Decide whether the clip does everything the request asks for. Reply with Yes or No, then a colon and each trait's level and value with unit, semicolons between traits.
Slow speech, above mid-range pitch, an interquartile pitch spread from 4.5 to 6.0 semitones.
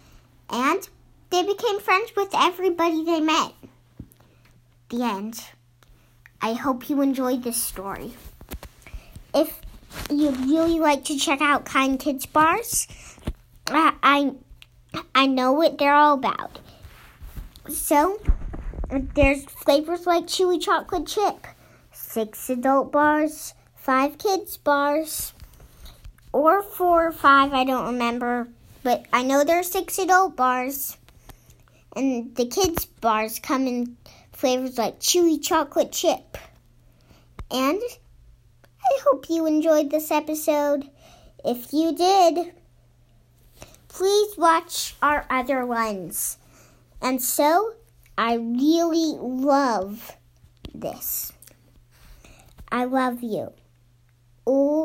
Yes: slow, 105 wpm; very high, 280 Hz; average, 5.2 semitones